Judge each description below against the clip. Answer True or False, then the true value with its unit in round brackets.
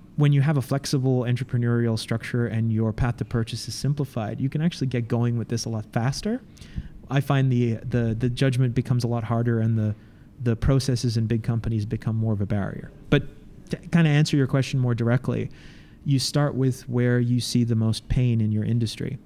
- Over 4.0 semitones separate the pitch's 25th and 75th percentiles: False (3.0 semitones)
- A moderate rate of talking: False (210 wpm)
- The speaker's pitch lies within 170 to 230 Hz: False (120 Hz)